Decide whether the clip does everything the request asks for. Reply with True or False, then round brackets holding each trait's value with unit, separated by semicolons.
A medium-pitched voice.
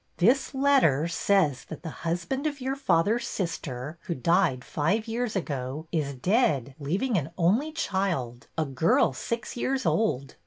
True (175 Hz)